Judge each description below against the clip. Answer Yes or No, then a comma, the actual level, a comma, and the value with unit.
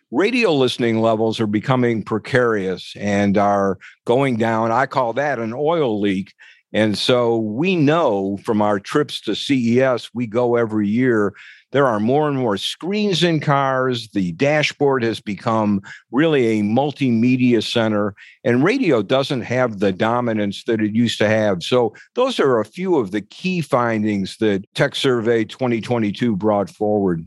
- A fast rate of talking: No, average, 155 wpm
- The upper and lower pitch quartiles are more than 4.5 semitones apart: No, average, 3.9 semitones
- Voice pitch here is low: Yes, low, 115 Hz